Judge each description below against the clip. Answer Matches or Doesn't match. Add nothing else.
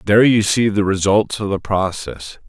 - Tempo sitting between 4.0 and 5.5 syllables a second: Matches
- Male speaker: Matches